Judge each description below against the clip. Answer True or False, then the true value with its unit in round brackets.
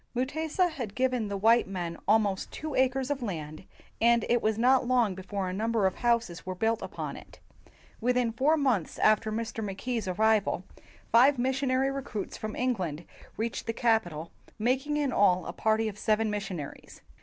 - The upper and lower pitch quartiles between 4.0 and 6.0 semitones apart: True (4.3 semitones)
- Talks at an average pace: True (175 wpm)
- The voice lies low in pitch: False (225 Hz)